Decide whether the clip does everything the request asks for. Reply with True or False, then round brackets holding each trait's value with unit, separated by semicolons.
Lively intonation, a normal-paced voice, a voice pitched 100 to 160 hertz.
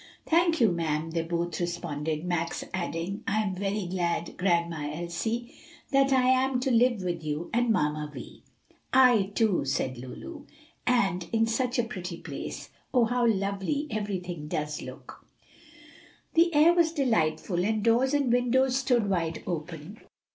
False (6.5 semitones; 150 wpm; 195 Hz)